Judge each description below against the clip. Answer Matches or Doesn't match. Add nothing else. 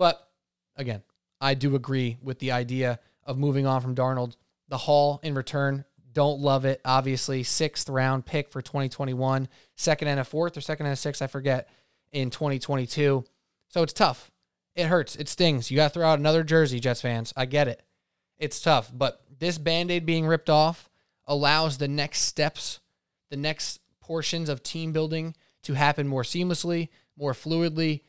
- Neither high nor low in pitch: Matches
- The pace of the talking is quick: Doesn't match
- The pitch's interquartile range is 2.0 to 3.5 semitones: Matches